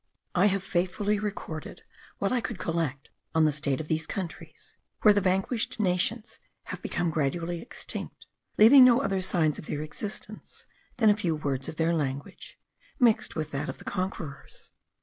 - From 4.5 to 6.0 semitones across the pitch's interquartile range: Yes, average, 4.9 semitones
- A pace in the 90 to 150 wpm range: No, average, 170 wpm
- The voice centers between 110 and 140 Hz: No, medium, 175 Hz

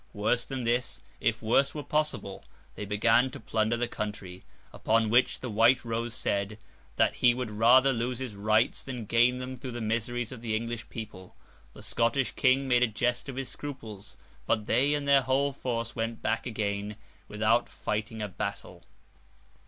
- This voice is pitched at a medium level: No, low, 115 Hz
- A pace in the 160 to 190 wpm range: Yes, average, 175 wpm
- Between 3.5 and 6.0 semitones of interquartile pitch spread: No, average, 2.8 semitones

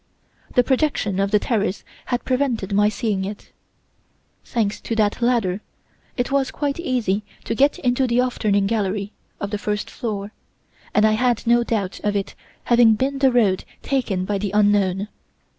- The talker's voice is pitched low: No, high, 215 Hz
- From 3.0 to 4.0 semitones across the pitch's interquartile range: Yes, average, 3.5 semitones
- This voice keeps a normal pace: Yes, average, 170 wpm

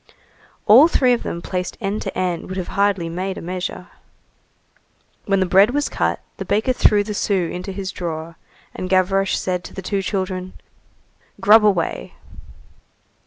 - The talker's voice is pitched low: No, high, 190 Hz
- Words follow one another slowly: No, average, 165 wpm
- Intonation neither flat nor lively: No, narrow, 2.1 semitones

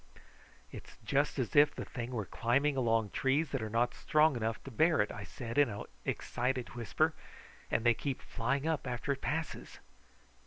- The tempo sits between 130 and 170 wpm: No, average, 185 wpm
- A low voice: Yes, low, 125 Hz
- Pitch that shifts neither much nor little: Yes, average, 3.8 semitones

